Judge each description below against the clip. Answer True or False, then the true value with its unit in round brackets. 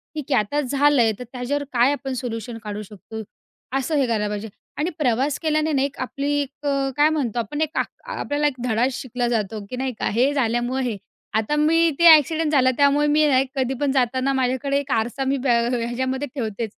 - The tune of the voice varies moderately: True (3.4 semitones)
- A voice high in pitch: True (260 Hz)